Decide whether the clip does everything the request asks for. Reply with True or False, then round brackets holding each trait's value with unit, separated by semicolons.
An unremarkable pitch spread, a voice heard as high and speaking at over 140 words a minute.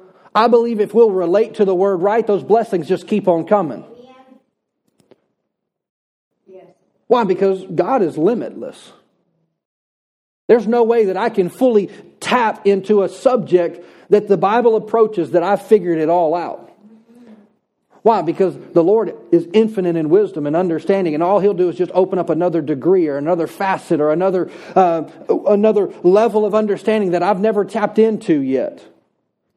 True (3.5 semitones; 200 Hz; 155 wpm)